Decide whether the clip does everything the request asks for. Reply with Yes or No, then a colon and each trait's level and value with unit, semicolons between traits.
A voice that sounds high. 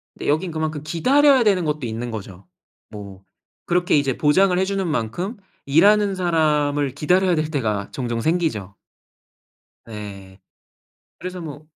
No: medium, 155 Hz